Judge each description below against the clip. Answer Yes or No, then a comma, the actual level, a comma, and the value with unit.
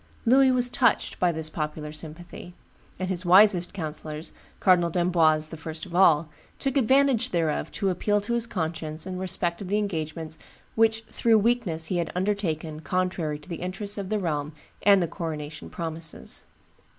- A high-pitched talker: No, medium, 175 Hz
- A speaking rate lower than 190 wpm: Yes, average, 165 wpm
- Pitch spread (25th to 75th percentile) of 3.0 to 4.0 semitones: No, average, 4.4 semitones